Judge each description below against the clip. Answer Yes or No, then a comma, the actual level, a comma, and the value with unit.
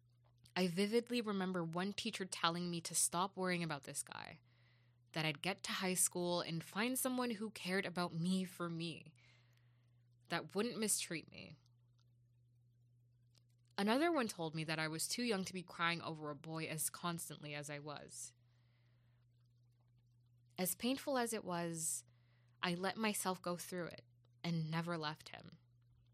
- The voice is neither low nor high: Yes, medium, 160 Hz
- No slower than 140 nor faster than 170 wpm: Yes, average, 155 wpm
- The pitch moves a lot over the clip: Yes, wide, 7.2 semitones